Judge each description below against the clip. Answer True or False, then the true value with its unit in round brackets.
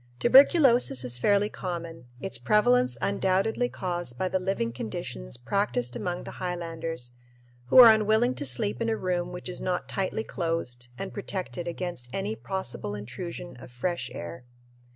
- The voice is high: False (175 Hz)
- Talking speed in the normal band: True (150 wpm)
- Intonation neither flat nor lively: False (7.8 semitones)